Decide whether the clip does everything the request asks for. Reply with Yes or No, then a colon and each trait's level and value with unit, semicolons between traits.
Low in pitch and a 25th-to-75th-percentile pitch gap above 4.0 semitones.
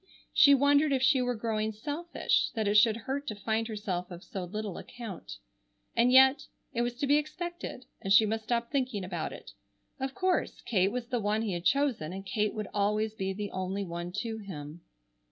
No: high, 220 Hz; average, 4.7 semitones